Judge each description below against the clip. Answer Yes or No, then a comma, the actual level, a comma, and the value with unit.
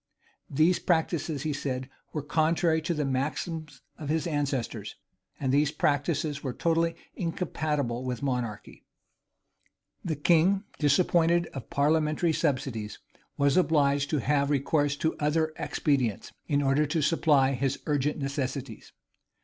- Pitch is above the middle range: No, medium, 145 Hz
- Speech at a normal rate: No, slow, 125 wpm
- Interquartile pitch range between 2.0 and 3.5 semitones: Yes, average, 2.7 semitones